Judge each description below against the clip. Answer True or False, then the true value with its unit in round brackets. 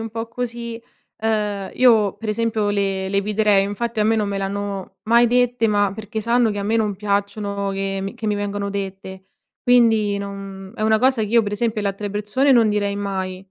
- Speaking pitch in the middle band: False (210 Hz)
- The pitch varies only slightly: True (2.1 semitones)